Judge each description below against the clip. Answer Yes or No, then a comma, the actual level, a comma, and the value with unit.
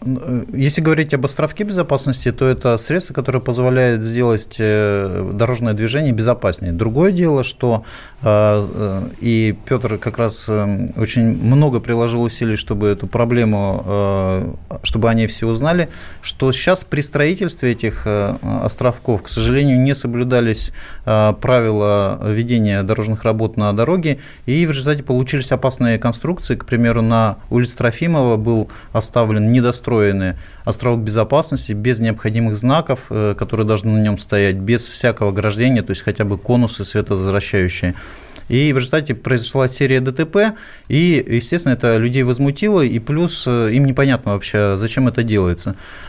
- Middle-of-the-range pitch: No, low, 115 Hz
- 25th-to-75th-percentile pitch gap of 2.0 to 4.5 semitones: Yes, average, 3.6 semitones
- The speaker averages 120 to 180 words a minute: Yes, average, 130 wpm